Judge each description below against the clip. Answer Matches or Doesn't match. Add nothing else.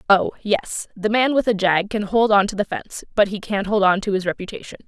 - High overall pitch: Matches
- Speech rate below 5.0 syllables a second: Doesn't match